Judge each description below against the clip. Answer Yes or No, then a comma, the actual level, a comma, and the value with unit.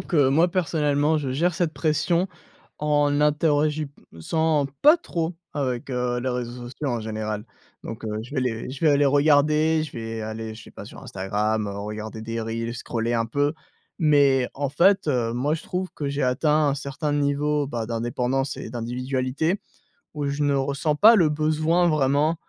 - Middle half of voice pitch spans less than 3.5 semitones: No, average, 4.2 semitones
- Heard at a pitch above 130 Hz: Yes, medium, 140 Hz